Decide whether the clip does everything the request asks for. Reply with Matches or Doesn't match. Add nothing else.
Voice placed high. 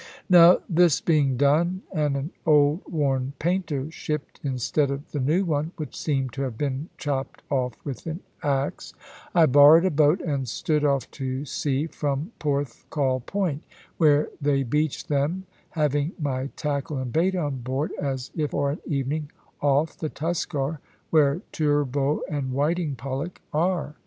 Doesn't match